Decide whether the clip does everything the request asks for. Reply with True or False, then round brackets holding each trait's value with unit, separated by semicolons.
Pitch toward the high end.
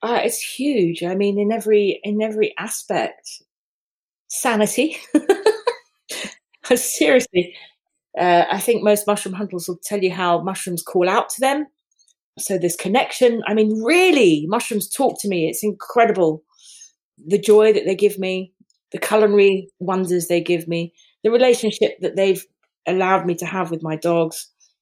True (205 Hz)